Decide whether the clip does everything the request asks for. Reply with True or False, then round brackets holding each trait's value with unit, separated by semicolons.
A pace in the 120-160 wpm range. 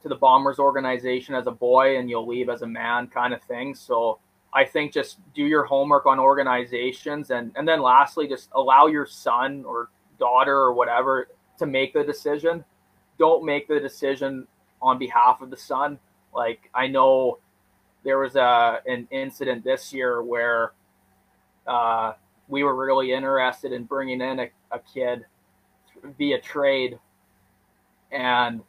True (155 wpm)